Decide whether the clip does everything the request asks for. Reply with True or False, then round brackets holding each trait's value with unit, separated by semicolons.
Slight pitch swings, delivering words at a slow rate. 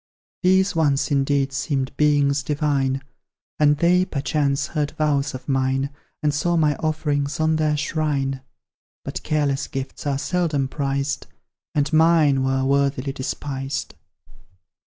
True (2.0 semitones; 125 wpm)